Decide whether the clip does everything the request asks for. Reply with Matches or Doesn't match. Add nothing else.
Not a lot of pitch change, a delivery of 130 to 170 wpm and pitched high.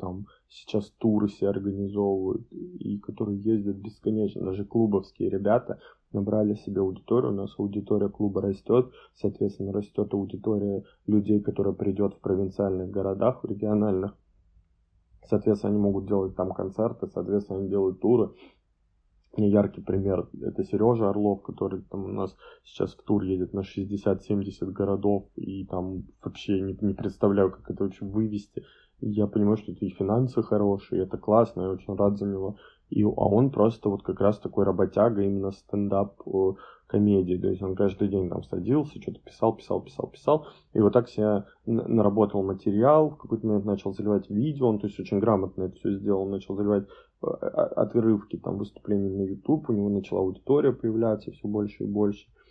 Doesn't match